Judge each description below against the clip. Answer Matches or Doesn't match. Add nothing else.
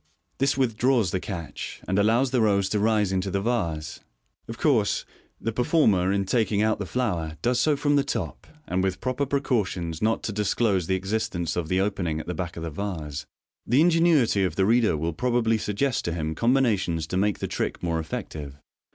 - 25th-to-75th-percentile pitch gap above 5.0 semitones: Matches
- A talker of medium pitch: Doesn't match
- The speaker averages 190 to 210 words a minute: Matches